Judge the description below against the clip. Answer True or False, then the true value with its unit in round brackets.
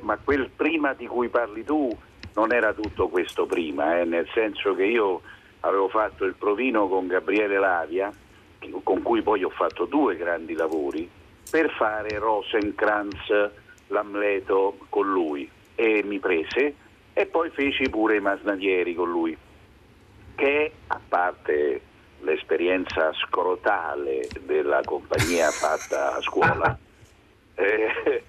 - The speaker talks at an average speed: True (125 wpm)